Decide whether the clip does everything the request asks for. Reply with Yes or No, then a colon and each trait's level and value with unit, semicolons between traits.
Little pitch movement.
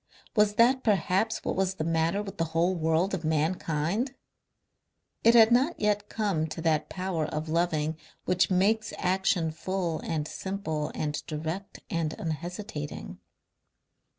No: average, 4.2 semitones